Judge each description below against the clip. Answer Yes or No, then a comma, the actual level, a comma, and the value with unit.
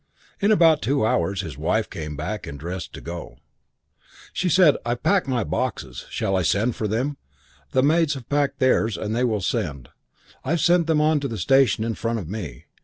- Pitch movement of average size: No, wide, 7.1 semitones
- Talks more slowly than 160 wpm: No, average, 195 wpm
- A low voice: Yes, low, 120 Hz